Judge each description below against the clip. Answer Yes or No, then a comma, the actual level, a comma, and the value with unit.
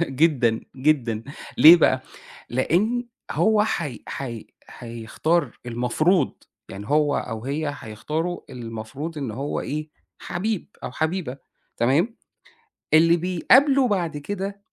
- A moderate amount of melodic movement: No, wide, 6.2 semitones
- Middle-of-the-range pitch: Yes, medium, 150 Hz